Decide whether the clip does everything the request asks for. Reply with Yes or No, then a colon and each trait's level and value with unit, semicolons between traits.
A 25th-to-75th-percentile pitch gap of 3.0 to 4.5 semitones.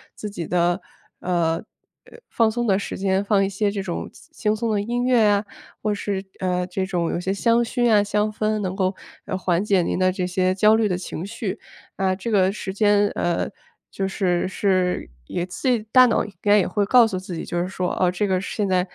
No: narrow, 2.5 semitones